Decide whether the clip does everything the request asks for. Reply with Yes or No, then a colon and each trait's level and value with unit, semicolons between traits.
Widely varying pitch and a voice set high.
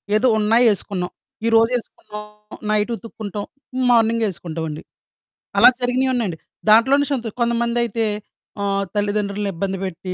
No: average, 3.0 semitones; high, 215 Hz